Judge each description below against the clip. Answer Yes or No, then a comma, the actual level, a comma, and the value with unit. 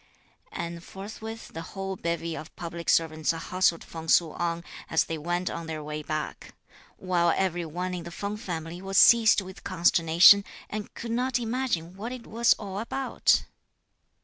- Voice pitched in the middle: Yes, medium, 175 Hz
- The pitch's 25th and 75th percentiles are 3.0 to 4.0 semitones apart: Yes, average, 3.6 semitones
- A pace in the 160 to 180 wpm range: Yes, average, 165 wpm